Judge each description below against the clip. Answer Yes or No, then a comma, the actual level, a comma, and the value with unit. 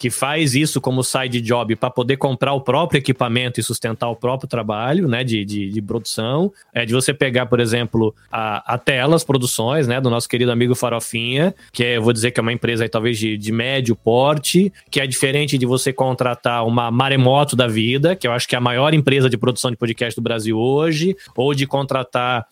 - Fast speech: Yes, fast, 215 wpm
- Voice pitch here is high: No, low, 125 Hz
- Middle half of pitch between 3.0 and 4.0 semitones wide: No, narrow, 2.6 semitones